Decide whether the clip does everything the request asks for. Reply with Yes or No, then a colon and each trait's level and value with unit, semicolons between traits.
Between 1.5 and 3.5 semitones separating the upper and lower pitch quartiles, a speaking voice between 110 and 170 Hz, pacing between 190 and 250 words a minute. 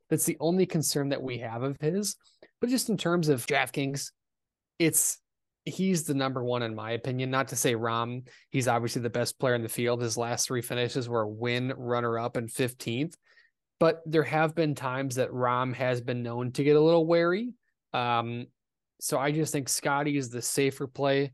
No: average, 4.4 semitones; low, 135 Hz; average, 200 wpm